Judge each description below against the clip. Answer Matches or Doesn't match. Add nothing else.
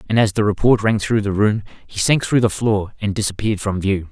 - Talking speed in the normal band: Doesn't match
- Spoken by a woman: Doesn't match